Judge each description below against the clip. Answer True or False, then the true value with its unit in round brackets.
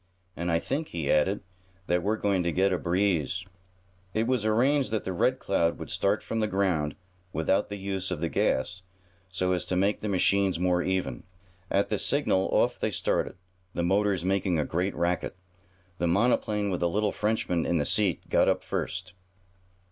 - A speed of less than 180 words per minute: False (185 wpm)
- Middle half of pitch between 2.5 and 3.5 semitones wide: True (2.9 semitones)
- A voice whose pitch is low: True (95 Hz)